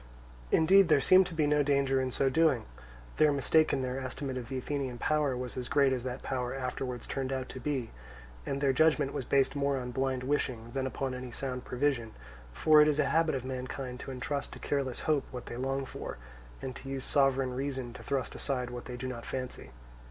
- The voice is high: No, low, 135 Hz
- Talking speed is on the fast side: Yes, fast, 220 wpm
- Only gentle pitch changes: Yes, narrow, 1.9 semitones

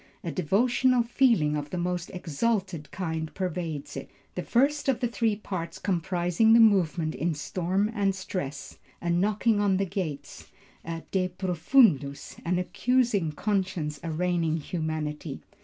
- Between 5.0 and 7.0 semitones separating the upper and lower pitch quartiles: No, average, 4.4 semitones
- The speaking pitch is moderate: Yes, medium, 180 Hz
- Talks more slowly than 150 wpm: Yes, average, 140 wpm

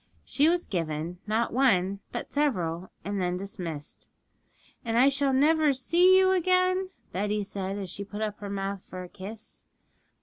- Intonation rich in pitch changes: Yes, wide, 7.2 semitones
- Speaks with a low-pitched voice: No, high, 210 Hz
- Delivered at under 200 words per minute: Yes, average, 170 wpm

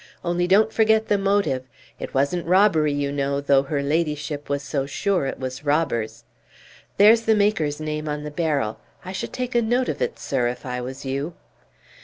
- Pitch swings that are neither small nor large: No, wide, 5.7 semitones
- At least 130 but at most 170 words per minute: No, average, 190 wpm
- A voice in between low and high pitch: Yes, medium, 150 Hz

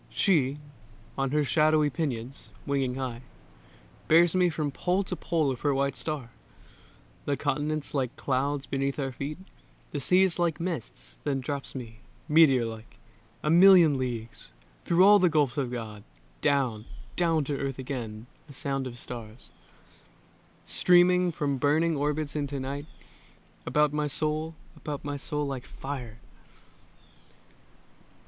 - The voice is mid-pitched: Yes, medium, 145 Hz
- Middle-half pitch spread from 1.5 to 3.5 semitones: Yes, average, 2.9 semitones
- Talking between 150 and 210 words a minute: No, average, 140 wpm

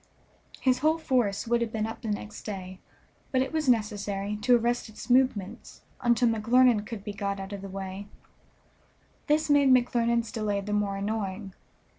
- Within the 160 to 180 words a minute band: Yes, average, 170 wpm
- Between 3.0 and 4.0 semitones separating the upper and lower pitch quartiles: Yes, average, 3.5 semitones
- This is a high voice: Yes, high, 220 Hz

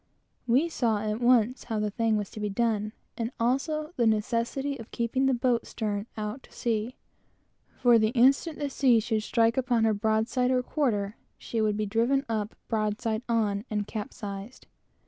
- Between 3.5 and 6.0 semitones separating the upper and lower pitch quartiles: No, average, 2.9 semitones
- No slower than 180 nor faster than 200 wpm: Yes, average, 185 wpm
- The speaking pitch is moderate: No, high, 230 Hz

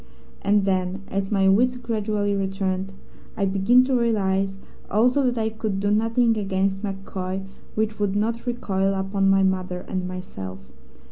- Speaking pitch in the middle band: No, high, 195 Hz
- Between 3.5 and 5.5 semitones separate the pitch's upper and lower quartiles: No, narrow, 2.4 semitones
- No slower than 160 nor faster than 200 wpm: No, average, 150 wpm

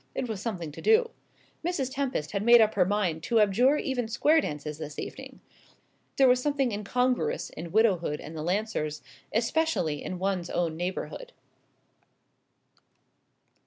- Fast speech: No, average, 145 wpm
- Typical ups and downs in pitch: No, wide, 7.0 semitones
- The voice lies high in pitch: Yes, high, 215 Hz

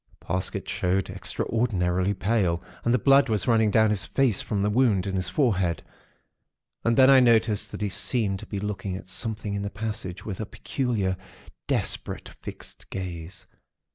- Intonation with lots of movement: No, average, 3.4 semitones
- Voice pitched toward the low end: Yes, low, 105 Hz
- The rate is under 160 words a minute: No, average, 170 wpm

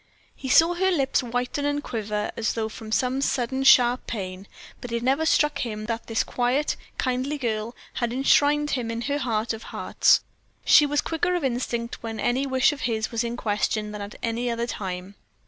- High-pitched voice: Yes, high, 245 Hz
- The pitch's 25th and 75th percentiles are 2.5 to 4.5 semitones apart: Yes, average, 3.6 semitones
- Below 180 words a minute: No, average, 195 wpm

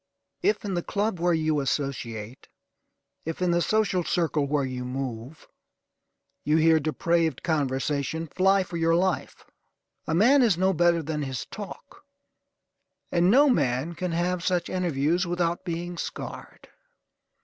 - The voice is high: No, medium, 170 Hz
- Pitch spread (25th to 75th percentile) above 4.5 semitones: No, average, 3.8 semitones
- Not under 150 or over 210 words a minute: No, average, 140 wpm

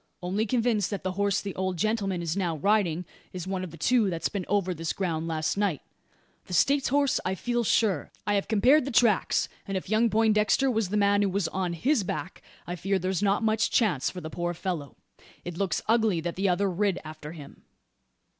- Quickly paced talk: Yes, fast, 210 wpm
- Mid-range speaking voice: No, high, 195 Hz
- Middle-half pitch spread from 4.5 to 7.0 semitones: No, average, 3.7 semitones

